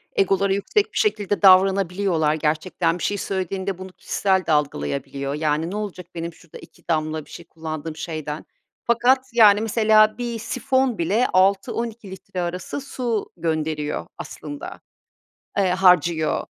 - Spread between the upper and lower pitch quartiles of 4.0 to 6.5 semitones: Yes, average, 4.9 semitones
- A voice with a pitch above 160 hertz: Yes, medium, 185 Hz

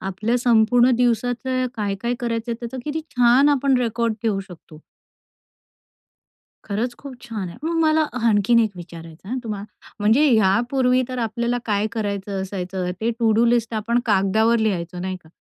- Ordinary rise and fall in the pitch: Yes, average, 3.5 semitones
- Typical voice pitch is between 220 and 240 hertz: Yes, high, 225 Hz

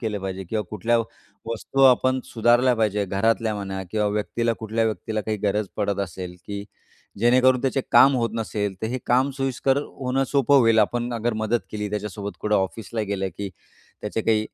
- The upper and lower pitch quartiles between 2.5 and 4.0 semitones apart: Yes, average, 2.8 semitones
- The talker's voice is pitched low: Yes, low, 110 Hz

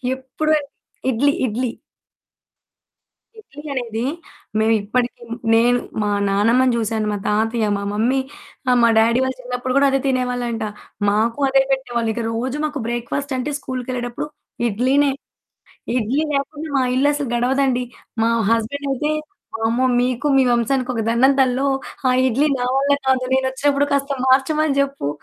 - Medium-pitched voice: No, very high, 255 Hz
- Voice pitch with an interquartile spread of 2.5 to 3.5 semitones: Yes, average, 2.9 semitones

